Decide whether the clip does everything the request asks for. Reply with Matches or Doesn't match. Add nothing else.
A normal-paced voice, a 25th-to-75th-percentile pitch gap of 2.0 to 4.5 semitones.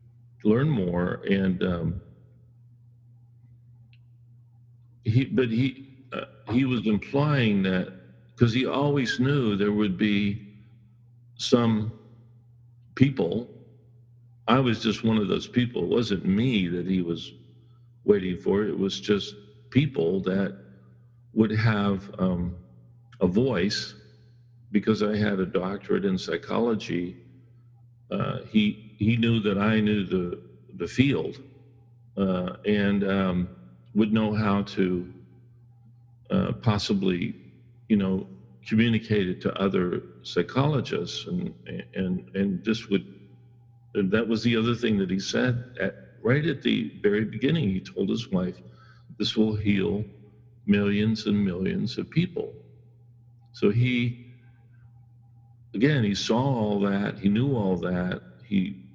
Doesn't match